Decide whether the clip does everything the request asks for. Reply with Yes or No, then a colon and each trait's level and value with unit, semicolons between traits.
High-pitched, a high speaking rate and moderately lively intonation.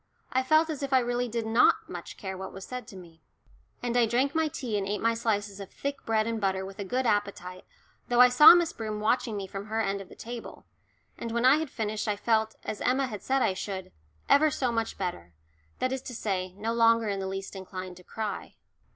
Yes: high, 220 Hz; fast, 235 wpm; average, 4.1 semitones